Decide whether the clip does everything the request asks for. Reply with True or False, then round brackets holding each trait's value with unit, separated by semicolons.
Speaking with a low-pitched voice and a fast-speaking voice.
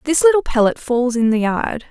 False (255 Hz; 220 wpm)